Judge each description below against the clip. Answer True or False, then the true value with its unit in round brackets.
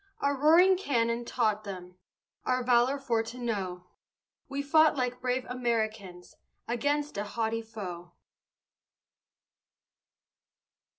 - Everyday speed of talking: False (105 wpm)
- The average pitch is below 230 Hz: False (235 Hz)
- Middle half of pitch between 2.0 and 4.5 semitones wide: True (4.2 semitones)